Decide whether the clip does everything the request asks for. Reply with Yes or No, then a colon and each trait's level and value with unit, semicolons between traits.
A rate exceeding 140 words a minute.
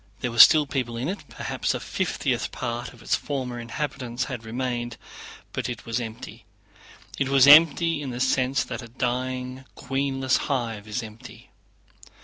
Yes: average, 160 wpm